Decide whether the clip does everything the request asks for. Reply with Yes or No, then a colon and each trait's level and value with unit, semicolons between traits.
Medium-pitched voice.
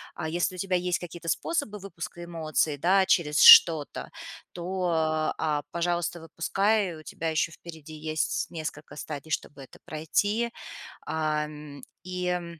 Yes: medium, 170 Hz